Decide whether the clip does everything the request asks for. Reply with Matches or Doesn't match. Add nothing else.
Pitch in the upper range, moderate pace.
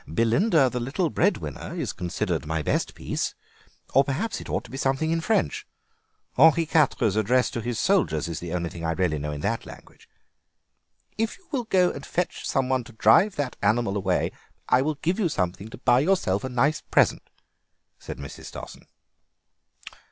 Doesn't match